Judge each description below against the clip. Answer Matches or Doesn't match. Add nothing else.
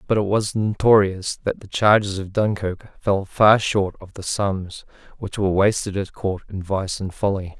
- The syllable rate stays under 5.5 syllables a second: Matches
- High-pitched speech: Doesn't match